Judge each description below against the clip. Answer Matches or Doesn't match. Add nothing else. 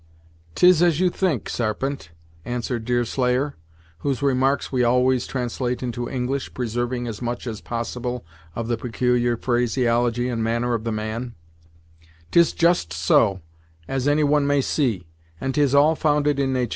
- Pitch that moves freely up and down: Doesn't match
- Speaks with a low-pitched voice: Matches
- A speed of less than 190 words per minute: Matches